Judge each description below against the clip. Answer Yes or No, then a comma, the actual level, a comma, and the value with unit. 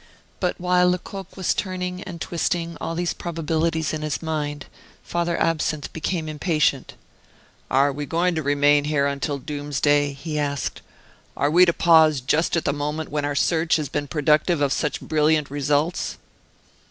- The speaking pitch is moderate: Yes, medium, 155 Hz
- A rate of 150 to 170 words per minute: Yes, average, 160 wpm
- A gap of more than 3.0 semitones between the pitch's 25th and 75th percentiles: No, narrow, 2.6 semitones